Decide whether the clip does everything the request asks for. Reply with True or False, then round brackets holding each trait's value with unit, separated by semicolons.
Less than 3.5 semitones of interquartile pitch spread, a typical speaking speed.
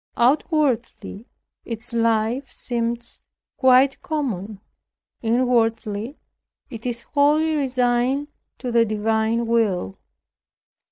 False (2.7 semitones; 80 wpm)